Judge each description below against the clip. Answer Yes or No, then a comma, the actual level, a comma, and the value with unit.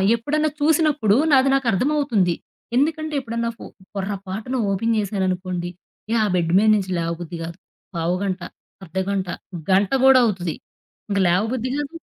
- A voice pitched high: Yes, high, 200 Hz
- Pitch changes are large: Yes, wide, 6.1 semitones